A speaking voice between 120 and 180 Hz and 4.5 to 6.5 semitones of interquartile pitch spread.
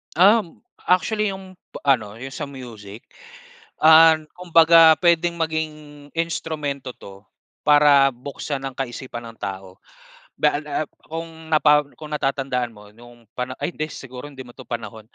Yes: medium, 140 Hz; average, 5.0 semitones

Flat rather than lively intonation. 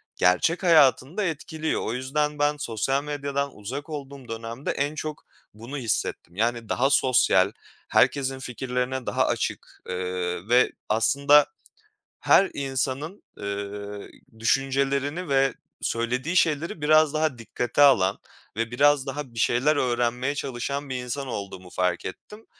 No: average, 4.0 semitones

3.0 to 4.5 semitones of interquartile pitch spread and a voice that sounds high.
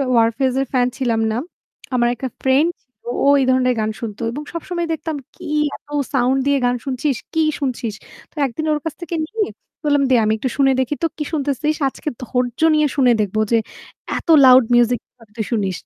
Yes: average, 3.6 semitones; very high, 260 Hz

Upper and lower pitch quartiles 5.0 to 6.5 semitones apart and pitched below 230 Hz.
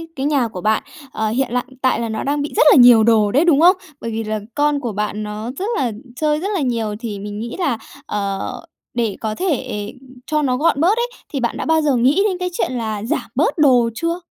No: wide, 5.4 semitones; high, 245 Hz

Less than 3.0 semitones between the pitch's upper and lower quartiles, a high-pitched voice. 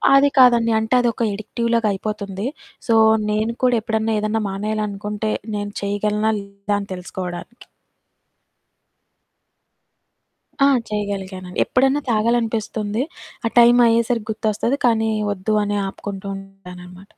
Yes: narrow, 2.5 semitones; high, 215 Hz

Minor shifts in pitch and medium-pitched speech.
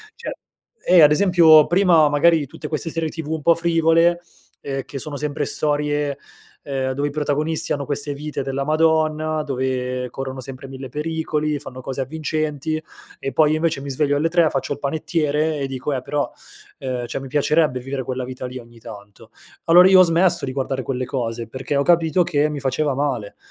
No: average, 3.0 semitones; medium, 145 Hz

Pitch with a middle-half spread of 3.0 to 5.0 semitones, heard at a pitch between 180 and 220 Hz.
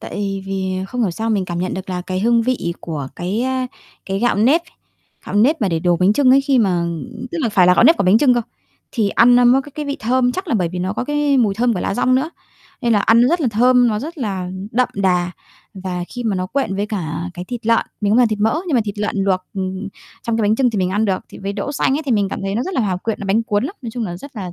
Yes: average, 4.7 semitones; high, 215 Hz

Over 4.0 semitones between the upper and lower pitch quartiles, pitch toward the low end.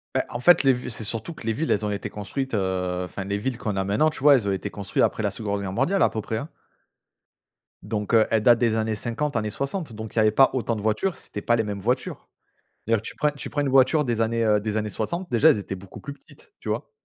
Yes: average, 4.4 semitones; low, 110 Hz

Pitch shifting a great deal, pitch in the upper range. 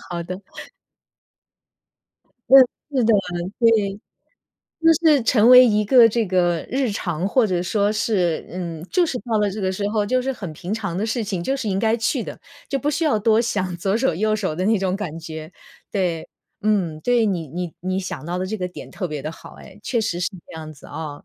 No: average, 4.3 semitones; high, 200 Hz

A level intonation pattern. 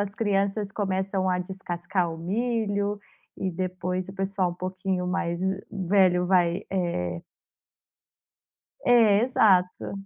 Yes: narrow, 1.9 semitones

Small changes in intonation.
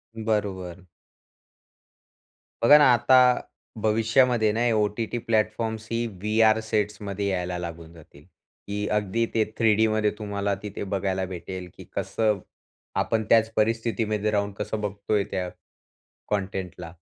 Yes: narrow, 2.3 semitones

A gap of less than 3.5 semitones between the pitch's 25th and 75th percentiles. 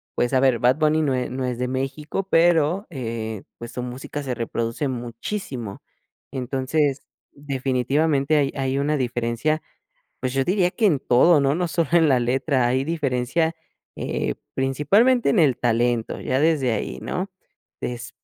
No: average, 4.0 semitones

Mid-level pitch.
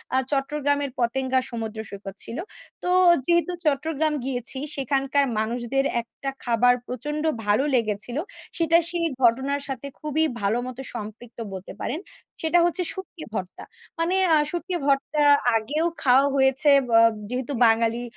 No: very high, 270 Hz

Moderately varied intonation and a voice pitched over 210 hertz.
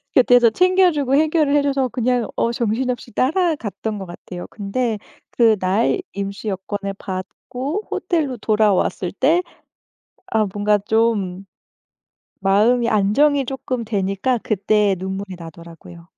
Yes: average, 4.8 semitones; high, 220 Hz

